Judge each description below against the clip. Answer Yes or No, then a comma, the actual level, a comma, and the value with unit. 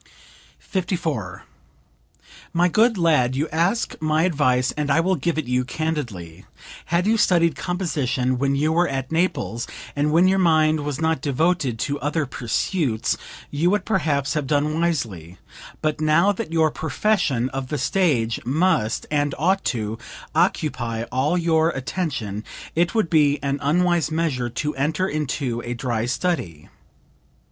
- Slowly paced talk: No, average, 150 wpm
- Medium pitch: Yes, medium, 150 Hz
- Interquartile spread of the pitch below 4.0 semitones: No, average, 4.8 semitones